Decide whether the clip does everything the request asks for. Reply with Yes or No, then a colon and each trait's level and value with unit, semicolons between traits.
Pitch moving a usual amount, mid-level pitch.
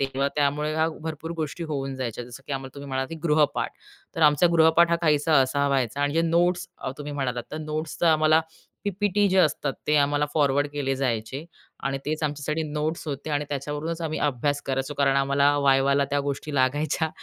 No: narrow, 2.3 semitones; medium, 145 Hz